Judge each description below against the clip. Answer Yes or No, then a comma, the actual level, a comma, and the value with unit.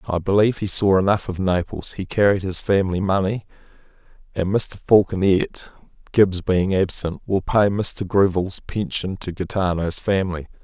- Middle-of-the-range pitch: No, very low, 95 Hz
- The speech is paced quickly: No, average, 145 wpm